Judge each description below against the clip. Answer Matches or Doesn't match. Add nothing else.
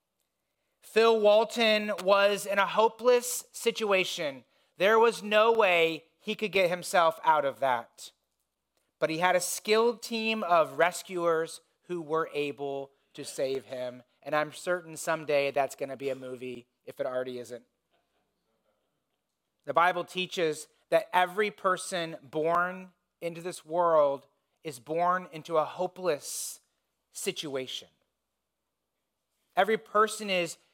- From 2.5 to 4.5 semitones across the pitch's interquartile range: Doesn't match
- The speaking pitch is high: Doesn't match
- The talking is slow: Matches